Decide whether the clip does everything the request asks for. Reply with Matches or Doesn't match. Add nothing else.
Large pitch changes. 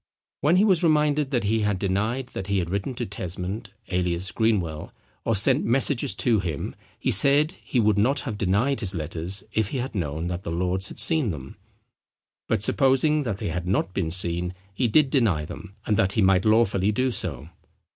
Matches